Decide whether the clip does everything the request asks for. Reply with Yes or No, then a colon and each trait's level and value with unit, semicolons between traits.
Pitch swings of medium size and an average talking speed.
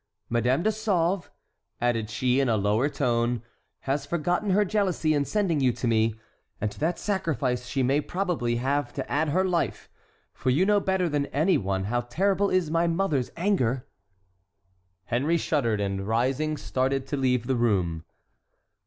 No: wide, 6.2 semitones; average, 165 wpm